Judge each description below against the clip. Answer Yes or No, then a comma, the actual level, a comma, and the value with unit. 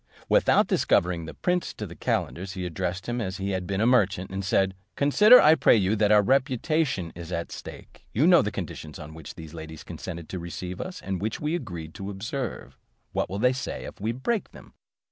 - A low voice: Yes, low, 100 Hz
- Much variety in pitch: Yes, wide, 6.2 semitones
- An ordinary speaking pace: No, fast, 225 wpm